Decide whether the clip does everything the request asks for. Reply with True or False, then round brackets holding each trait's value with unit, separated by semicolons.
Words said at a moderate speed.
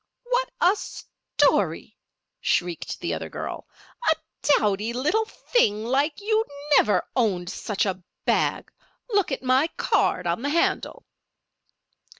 False (125 wpm)